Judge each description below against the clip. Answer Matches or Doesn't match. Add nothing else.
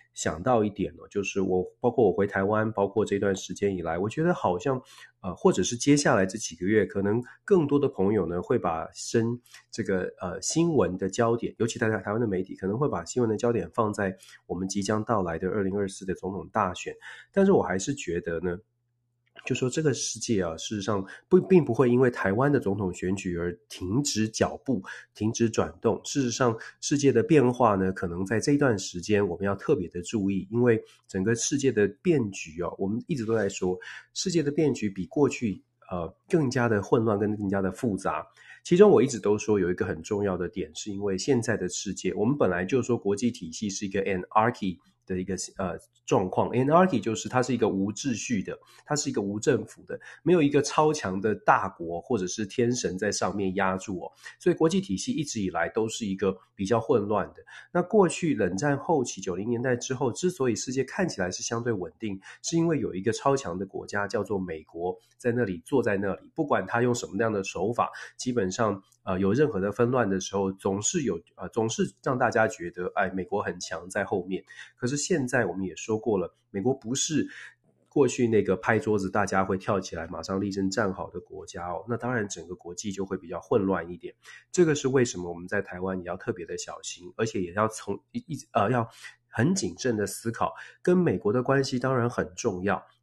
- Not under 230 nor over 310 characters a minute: Doesn't match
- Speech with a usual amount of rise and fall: Matches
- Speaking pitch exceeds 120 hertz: Doesn't match